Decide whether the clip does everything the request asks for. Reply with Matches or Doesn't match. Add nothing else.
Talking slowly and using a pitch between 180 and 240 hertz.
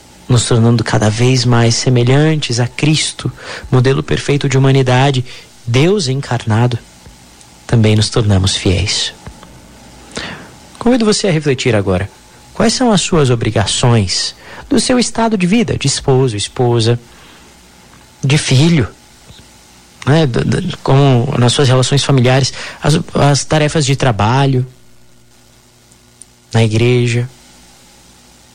Doesn't match